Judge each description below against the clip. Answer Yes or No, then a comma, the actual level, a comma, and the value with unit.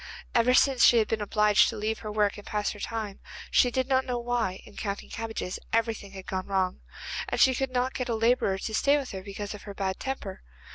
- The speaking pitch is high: Yes, high, 220 Hz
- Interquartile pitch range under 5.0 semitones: Yes, average, 3.4 semitones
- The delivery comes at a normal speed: No, fast, 235 wpm